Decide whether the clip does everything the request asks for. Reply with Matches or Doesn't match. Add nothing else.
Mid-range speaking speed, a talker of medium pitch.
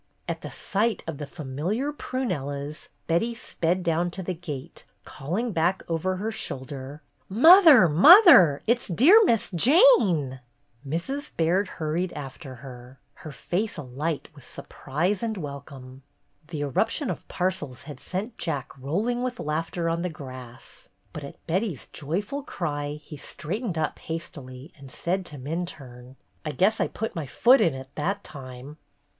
Matches